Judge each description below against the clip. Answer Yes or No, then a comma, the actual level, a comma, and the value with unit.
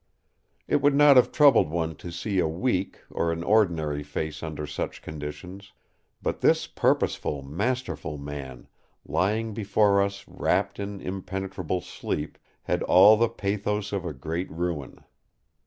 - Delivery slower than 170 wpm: Yes, average, 140 wpm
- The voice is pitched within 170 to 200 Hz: No, very low, 90 Hz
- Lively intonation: No, average, 4.8 semitones